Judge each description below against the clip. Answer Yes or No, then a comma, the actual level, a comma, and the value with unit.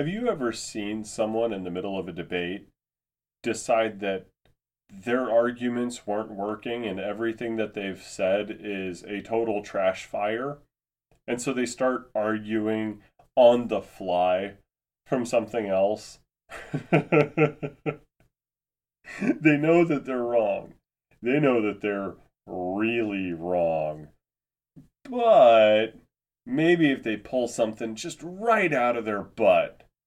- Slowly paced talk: Yes, slow, 120 wpm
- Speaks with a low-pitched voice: Yes, low, 110 Hz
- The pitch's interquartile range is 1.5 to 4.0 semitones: No, average, 4.4 semitones